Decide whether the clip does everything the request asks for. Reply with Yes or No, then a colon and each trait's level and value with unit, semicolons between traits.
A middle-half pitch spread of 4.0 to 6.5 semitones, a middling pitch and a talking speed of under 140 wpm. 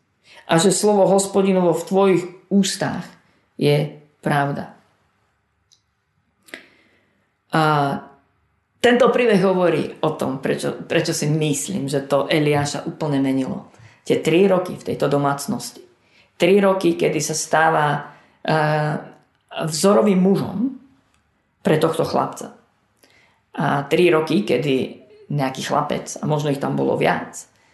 Yes: average, 4.9 semitones; medium, 155 Hz; average, 115 wpm